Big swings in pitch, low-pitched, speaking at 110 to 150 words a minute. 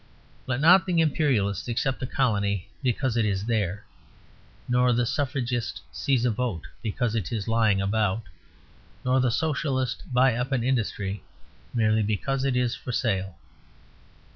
No: average, 3.7 semitones; low, 120 Hz; average, 145 wpm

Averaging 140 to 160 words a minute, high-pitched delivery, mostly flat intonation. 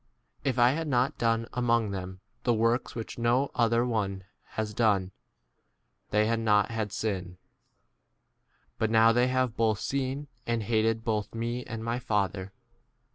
No: average, 155 wpm; low, 115 Hz; narrow, 2.3 semitones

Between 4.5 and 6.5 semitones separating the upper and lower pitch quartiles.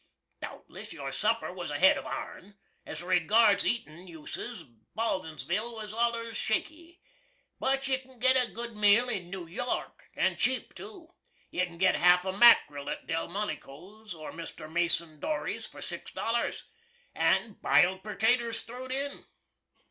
Yes: average, 5.2 semitones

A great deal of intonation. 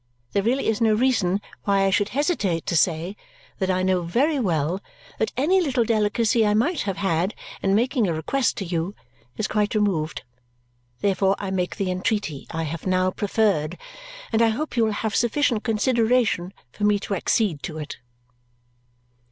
No: average, 3.8 semitones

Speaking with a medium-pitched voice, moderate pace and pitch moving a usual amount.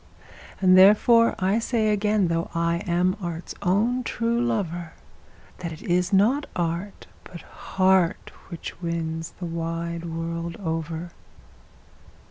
No: medium, 175 Hz; slow, 120 wpm; average, 3.4 semitones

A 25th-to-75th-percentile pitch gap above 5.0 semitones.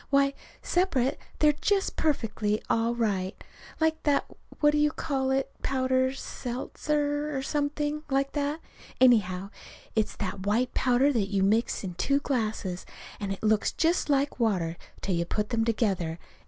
Yes: wide, 5.6 semitones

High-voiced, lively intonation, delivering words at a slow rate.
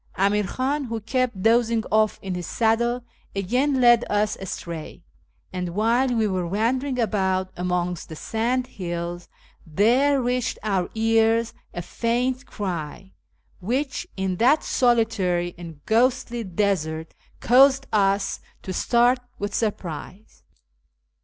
No: high, 220 Hz; average, 4.9 semitones; slow, 120 wpm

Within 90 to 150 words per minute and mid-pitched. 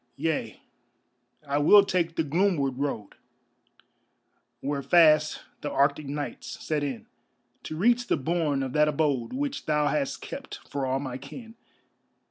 Yes: average, 140 wpm; medium, 150 Hz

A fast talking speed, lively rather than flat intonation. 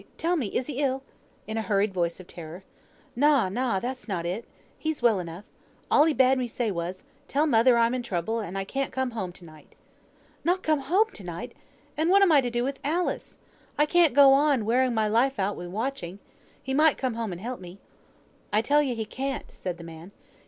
Yes: fast, 215 wpm; wide, 6.1 semitones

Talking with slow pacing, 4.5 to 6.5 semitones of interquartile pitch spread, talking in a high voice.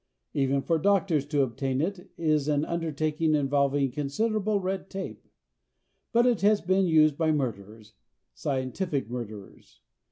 No: slow, 130 wpm; wide, 5.4 semitones; medium, 150 Hz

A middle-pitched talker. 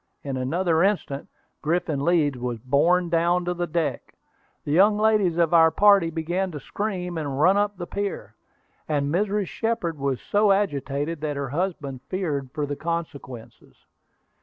Yes: medium, 165 Hz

